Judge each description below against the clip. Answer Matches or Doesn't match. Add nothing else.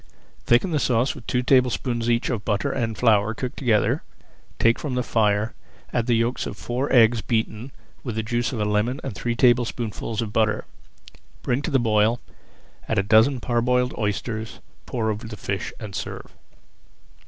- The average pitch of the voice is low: Matches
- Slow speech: Doesn't match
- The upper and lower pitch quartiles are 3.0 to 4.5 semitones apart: Doesn't match